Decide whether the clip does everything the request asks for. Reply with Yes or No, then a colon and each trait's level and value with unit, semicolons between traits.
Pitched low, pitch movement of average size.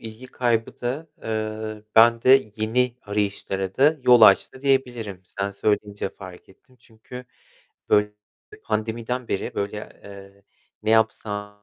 Yes: low, 110 Hz; average, 3.1 semitones